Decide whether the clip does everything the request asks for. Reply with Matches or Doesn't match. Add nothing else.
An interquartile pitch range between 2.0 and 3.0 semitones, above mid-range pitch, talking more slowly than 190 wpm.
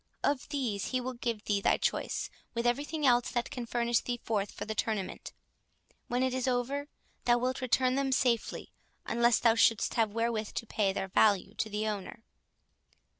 Matches